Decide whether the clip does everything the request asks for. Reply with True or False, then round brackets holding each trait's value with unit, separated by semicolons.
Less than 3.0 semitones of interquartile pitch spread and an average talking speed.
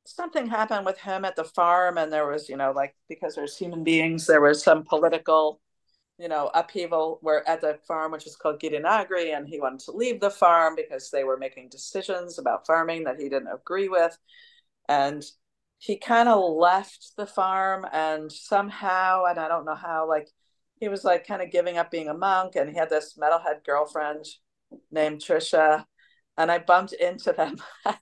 False (3.8 semitones; 190 wpm)